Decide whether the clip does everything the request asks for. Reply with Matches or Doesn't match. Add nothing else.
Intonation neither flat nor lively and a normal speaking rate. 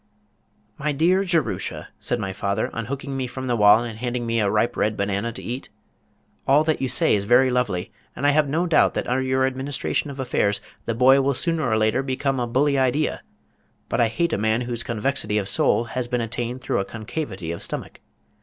Doesn't match